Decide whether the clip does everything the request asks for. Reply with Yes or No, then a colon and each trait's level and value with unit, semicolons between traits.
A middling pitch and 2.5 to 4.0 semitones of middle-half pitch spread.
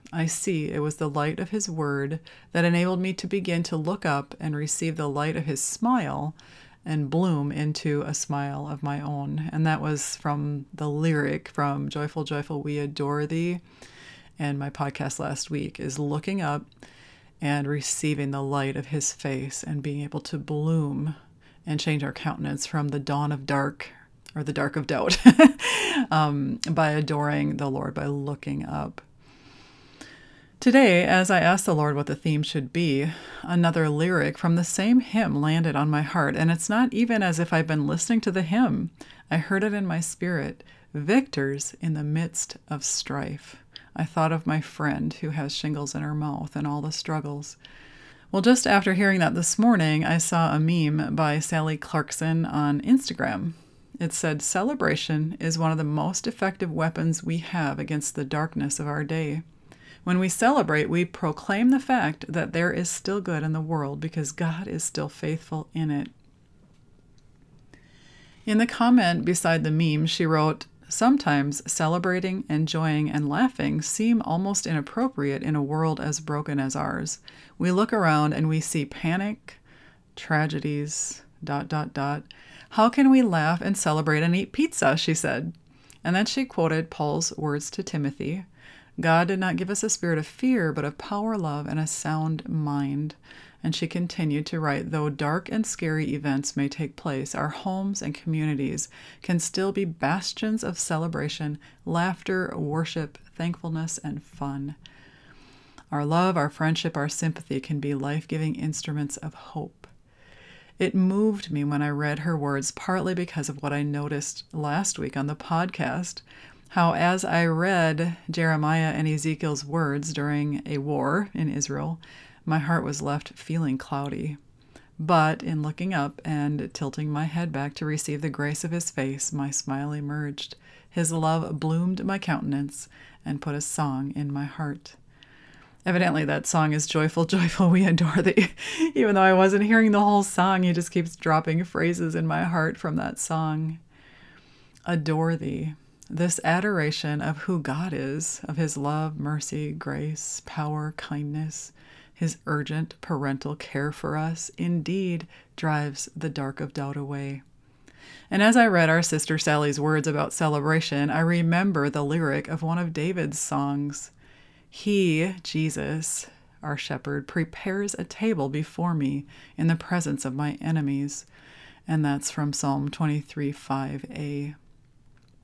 Yes: medium, 155 Hz; average, 2.8 semitones